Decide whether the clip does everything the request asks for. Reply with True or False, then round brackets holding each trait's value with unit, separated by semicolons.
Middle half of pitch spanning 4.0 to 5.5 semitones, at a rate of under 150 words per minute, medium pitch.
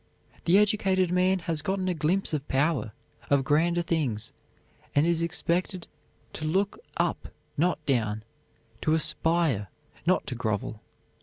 True (4.6 semitones; 140 wpm; 165 Hz)